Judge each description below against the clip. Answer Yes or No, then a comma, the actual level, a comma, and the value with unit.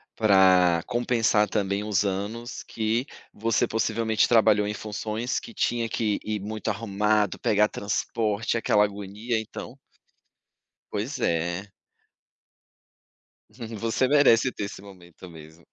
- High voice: No, low, 105 Hz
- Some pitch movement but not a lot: No, narrow, 2.3 semitones